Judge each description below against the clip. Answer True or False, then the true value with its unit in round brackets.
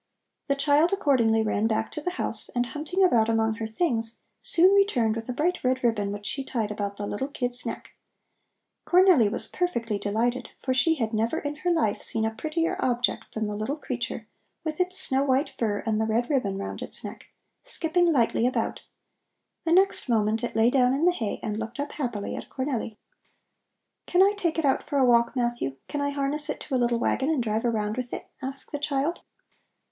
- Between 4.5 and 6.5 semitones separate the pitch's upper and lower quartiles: True (5.2 semitones)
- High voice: True (250 Hz)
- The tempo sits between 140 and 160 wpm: False (205 wpm)